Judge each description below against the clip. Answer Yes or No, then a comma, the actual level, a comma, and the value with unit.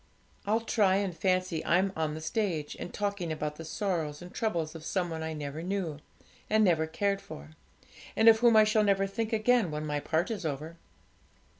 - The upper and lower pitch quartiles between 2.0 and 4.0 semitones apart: No, average, 4.4 semitones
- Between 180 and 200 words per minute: Yes, average, 195 wpm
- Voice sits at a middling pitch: Yes, medium, 180 Hz